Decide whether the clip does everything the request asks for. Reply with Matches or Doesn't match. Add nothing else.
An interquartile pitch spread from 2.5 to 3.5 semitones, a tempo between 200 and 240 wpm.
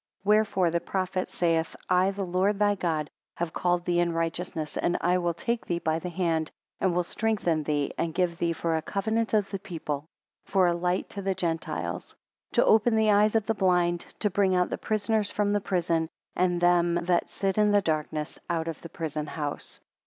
Matches